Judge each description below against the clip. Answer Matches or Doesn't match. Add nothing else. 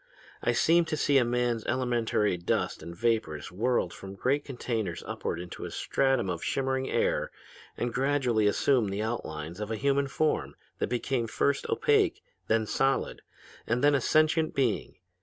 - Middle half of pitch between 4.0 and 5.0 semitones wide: Matches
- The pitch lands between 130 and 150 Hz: Doesn't match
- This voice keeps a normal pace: Matches